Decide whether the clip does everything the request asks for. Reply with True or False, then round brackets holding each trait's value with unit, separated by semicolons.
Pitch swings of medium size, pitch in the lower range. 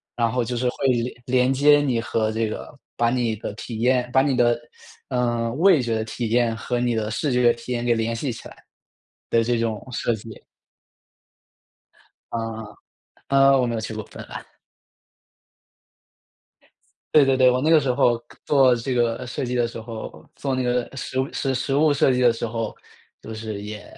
False (2.2 semitones; 120 Hz)